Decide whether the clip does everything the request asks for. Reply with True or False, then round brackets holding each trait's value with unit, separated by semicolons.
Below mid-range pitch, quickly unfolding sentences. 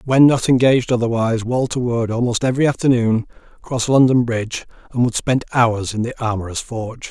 False (120 Hz; 170 wpm)